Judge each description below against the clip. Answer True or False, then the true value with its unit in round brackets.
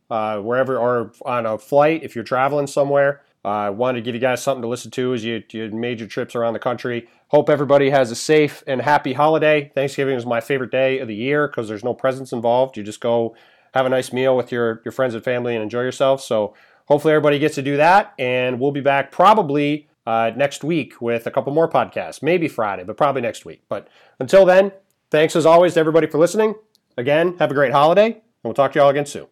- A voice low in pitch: True (130 Hz)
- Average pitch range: True (3.5 semitones)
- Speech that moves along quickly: True (235 wpm)